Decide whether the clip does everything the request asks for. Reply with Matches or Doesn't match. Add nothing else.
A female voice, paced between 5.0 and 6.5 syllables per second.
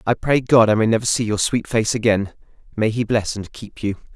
Doesn't match